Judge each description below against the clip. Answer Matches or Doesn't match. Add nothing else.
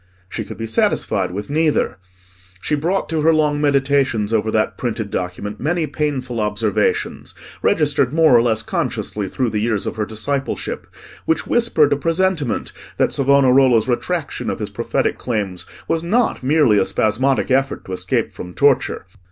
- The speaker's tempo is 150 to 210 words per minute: Matches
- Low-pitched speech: Matches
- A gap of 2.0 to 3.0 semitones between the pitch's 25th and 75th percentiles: Doesn't match